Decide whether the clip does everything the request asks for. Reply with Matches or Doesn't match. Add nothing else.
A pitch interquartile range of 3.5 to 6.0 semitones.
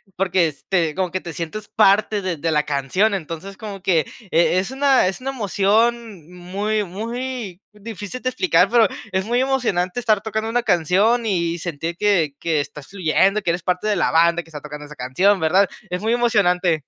Matches